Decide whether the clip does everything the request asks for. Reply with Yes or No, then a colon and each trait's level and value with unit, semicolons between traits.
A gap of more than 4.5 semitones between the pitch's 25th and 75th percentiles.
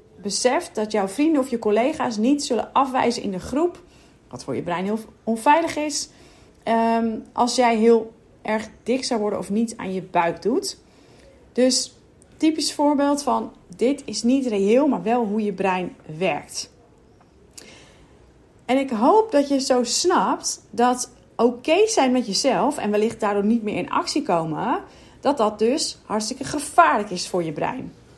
Yes: average, 4.9 semitones